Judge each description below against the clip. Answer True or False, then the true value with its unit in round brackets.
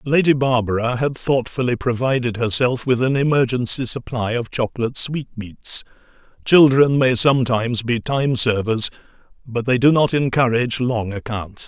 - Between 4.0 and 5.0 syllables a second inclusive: True (4.9 syllables/s)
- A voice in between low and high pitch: False (125 Hz)